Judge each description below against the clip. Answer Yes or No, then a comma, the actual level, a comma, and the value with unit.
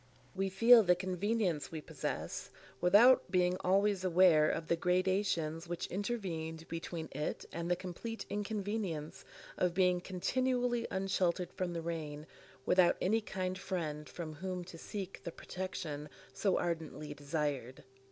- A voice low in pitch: No, medium, 180 Hz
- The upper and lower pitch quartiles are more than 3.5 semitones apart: No, average, 3.0 semitones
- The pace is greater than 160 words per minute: No, slow, 135 wpm